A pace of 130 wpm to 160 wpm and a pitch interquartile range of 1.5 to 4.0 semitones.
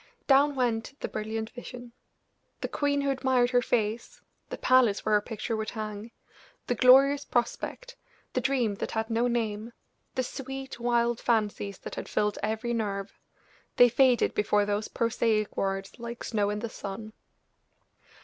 Yes: average, 155 wpm; average, 2.9 semitones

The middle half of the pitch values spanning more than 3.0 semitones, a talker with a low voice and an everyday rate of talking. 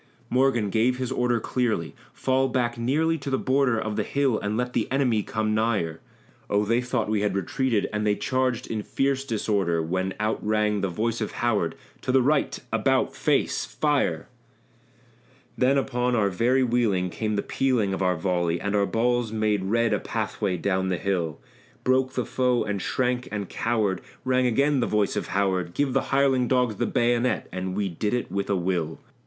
Yes: average, 4.2 semitones; low, 110 Hz; average, 190 wpm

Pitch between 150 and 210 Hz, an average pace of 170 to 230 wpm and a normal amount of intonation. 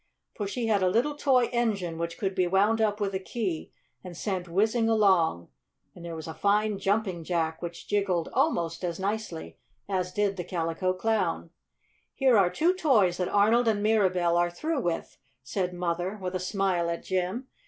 Yes: high, 190 Hz; average, 185 wpm; average, 3.7 semitones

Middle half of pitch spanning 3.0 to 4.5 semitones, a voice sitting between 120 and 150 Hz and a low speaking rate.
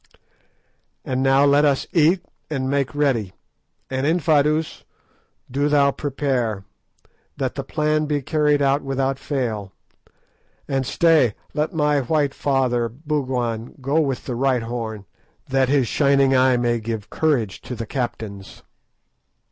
Yes: average, 3.3 semitones; low, 135 Hz; slow, 130 wpm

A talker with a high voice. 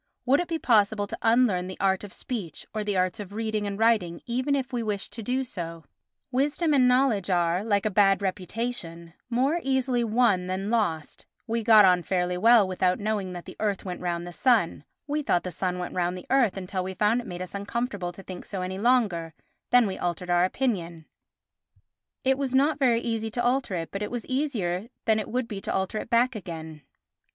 Yes: high, 205 Hz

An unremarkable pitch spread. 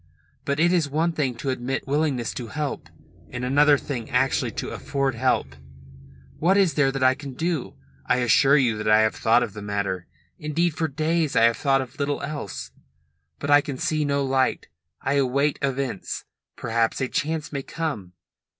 Yes: average, 3.5 semitones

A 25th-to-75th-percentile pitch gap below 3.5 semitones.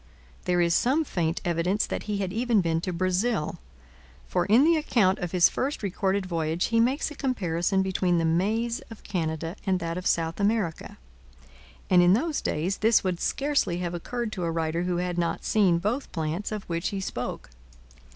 No: average, 4.3 semitones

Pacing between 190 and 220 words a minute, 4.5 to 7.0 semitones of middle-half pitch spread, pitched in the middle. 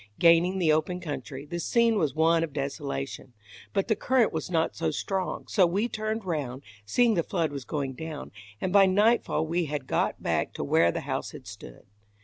Yes: average, 195 wpm; average, 5.1 semitones; medium, 165 Hz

